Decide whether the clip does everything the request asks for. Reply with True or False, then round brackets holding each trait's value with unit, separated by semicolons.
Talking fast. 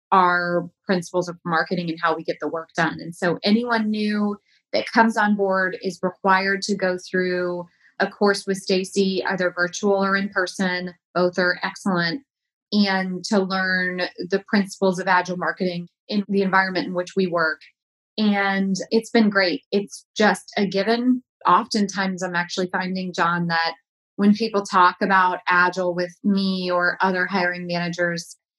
False (160 wpm)